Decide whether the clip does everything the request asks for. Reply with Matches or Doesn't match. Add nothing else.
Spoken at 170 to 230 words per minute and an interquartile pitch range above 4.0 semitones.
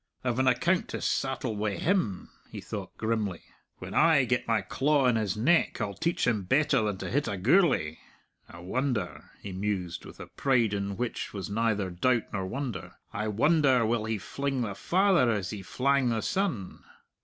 Matches